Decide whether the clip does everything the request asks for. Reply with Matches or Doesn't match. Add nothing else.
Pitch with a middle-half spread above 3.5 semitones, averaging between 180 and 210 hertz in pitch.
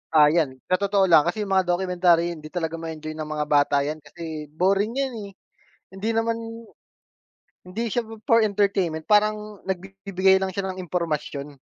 Matches